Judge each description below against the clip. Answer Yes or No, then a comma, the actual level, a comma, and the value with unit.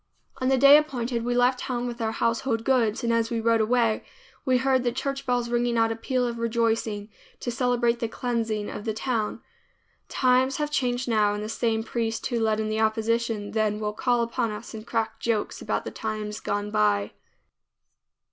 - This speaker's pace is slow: No, average, 195 wpm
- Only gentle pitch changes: Yes, narrow, 2.0 semitones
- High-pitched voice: Yes, high, 230 Hz